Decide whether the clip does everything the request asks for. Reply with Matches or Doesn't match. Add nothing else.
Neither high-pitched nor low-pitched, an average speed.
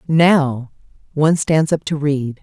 Matches